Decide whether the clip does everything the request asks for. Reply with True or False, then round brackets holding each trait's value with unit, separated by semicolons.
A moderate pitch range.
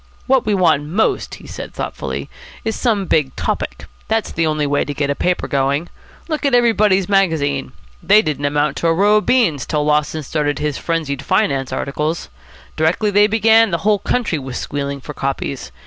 False (6.4 semitones)